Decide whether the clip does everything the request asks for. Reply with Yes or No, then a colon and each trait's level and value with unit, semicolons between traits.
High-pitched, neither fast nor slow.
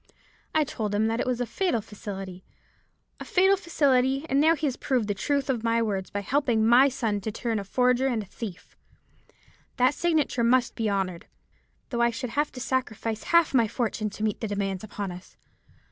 Yes: high, 235 Hz; average, 195 wpm